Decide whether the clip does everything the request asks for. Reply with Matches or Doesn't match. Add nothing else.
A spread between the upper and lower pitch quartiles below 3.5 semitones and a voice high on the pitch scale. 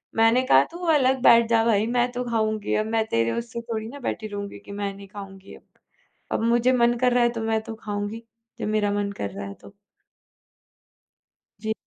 Matches